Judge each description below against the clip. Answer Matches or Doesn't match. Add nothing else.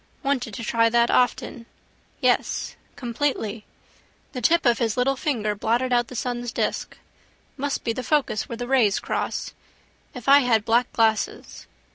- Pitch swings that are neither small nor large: Doesn't match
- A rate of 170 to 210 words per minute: Doesn't match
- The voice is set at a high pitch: Matches